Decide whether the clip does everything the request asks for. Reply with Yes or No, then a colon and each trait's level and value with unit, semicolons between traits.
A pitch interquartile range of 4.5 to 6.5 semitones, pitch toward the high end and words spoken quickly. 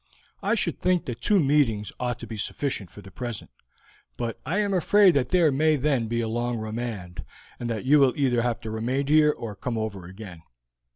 No: average, 5.2 semitones; low, 120 Hz; fast, 215 wpm